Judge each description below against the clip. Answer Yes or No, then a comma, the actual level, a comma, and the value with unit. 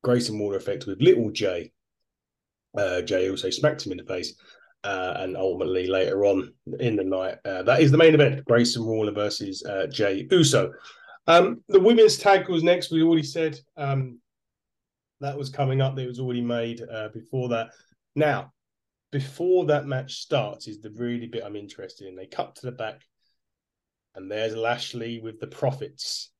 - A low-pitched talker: Yes, low, 120 Hz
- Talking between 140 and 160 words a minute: No, average, 175 wpm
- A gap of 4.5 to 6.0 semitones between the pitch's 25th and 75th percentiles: Yes, average, 5.2 semitones